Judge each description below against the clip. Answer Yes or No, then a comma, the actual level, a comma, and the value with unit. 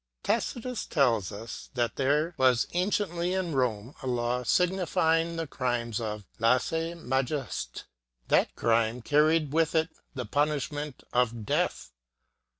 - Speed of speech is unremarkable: No, slow, 130 wpm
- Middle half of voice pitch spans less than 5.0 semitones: No, wide, 5.5 semitones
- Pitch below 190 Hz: Yes, medium, 140 Hz